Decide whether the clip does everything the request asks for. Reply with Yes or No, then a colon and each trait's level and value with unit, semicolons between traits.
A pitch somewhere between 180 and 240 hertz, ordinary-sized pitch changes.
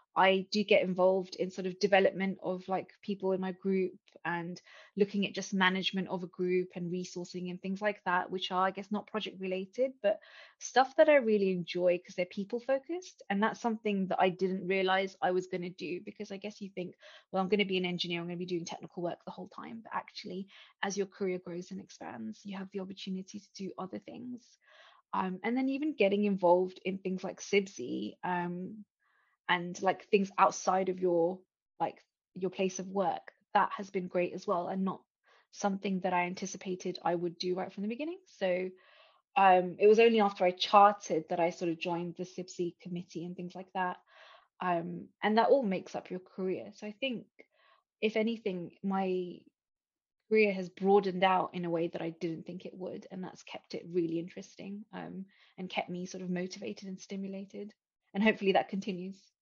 No: high, 190 Hz; narrow, 2.0 semitones